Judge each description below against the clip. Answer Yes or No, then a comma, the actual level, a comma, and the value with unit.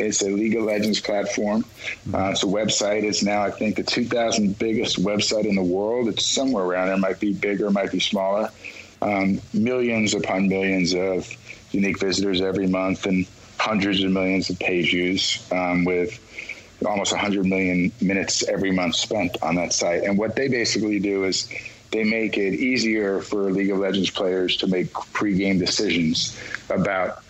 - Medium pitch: No, low, 100 Hz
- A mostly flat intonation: Yes, narrow, 2.0 semitones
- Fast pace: No, average, 175 wpm